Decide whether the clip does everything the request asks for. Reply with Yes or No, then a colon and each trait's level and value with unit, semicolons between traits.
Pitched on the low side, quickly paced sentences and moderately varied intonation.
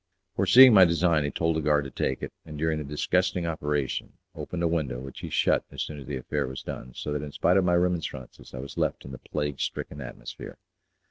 Yes: very low, 75 Hz; fast, 230 wpm; average, 3.7 semitones